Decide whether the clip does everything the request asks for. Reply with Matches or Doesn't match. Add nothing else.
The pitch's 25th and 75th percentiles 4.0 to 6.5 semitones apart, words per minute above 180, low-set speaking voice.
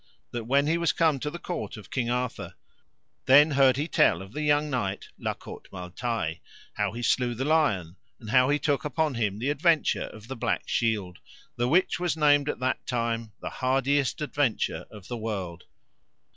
Matches